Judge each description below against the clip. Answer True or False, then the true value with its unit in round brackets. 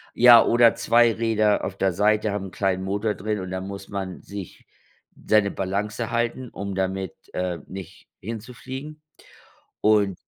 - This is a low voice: True (105 Hz)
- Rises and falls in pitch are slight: False (3.1 semitones)